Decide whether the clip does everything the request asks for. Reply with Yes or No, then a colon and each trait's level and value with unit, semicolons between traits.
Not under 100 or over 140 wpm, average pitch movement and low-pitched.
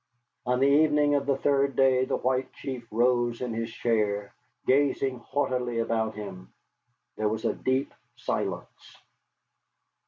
Yes: slow, 135 wpm; average, 3.1 semitones; low, 125 Hz